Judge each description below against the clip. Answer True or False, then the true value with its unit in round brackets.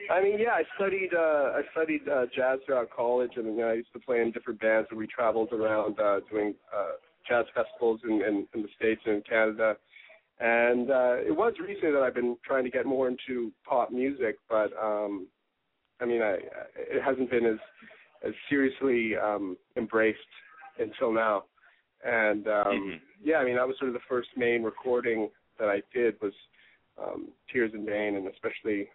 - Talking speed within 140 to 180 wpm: False (190 wpm)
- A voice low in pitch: True (115 Hz)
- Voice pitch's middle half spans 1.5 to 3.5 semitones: True (3.1 semitones)